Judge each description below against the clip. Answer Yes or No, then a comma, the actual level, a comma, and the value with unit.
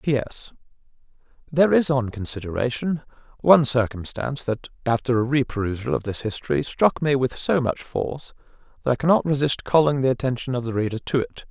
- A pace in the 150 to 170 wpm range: Yes, average, 165 wpm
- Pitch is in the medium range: No, low, 130 Hz